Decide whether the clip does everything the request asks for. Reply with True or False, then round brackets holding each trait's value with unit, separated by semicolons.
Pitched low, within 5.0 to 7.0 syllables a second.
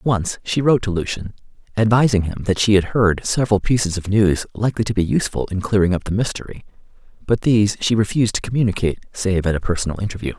True (100 Hz; 6.7 syllables/s)